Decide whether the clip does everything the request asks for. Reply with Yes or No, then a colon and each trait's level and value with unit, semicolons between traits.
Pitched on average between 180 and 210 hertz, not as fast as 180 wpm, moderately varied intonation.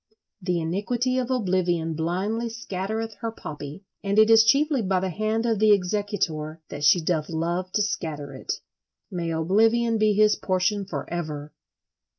Yes: high, 190 Hz; average, 160 wpm; average, 4.7 semitones